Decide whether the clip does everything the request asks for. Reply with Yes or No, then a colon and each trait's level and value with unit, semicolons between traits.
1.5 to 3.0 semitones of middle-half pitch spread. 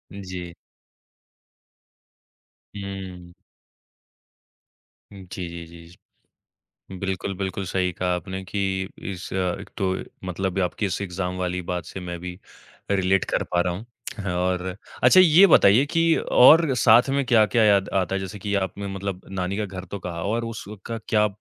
Yes: narrow, 2.6 semitones